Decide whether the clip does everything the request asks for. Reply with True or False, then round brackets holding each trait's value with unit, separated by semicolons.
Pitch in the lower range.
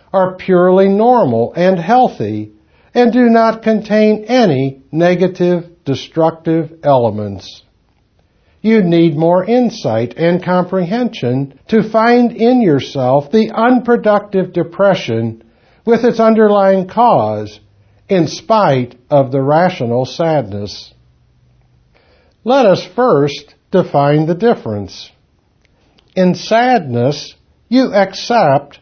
False (175 Hz)